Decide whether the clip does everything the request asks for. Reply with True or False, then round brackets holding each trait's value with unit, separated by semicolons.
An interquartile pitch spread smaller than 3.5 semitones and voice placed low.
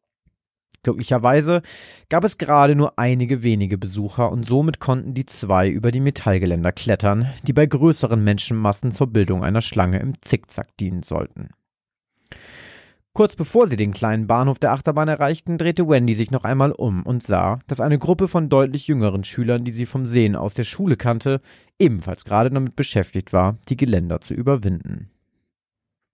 False (5.5 semitones; 120 Hz)